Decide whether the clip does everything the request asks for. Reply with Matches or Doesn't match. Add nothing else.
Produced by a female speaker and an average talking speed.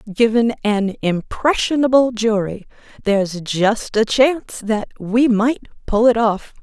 Doesn't match